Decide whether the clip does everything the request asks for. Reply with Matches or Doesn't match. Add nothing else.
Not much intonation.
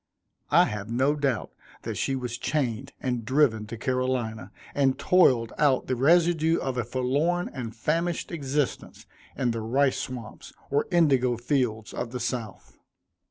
Doesn't match